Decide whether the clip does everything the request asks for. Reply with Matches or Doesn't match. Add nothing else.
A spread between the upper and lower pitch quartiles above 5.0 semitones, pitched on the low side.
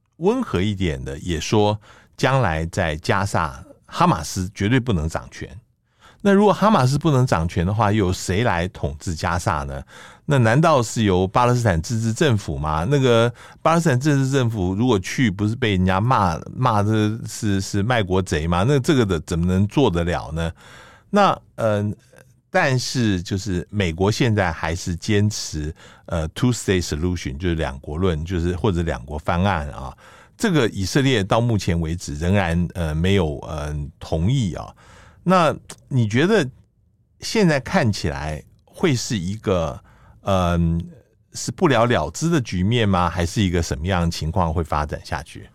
Matches